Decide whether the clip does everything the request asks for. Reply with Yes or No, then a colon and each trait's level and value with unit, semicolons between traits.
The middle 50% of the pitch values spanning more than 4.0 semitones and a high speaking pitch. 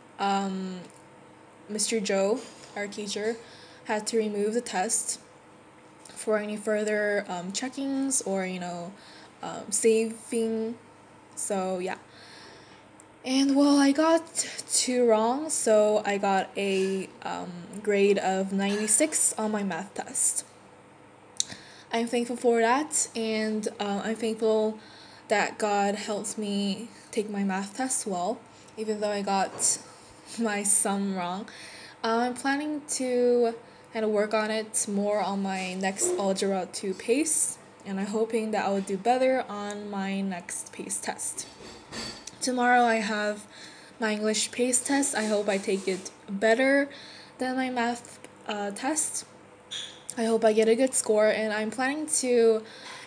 No: average, 2.8 semitones; high, 215 Hz